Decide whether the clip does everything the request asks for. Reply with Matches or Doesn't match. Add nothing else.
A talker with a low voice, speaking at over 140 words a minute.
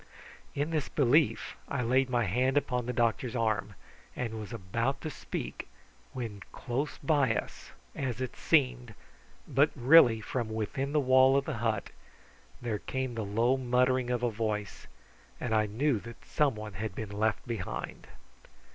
Matches